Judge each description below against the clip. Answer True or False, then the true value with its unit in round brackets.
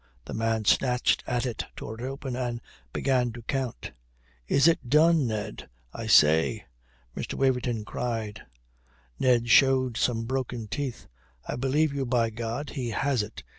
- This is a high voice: False (125 Hz)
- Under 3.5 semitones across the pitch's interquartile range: True (2.8 semitones)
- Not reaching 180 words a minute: True (150 wpm)